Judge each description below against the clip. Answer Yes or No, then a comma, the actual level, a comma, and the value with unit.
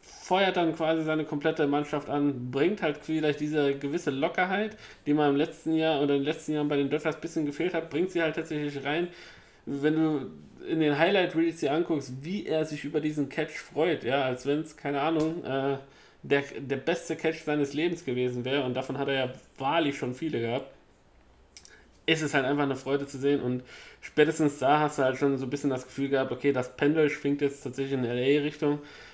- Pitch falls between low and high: Yes, medium, 145 Hz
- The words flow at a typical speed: No, fast, 210 wpm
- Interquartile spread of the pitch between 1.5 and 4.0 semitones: Yes, narrow, 2.5 semitones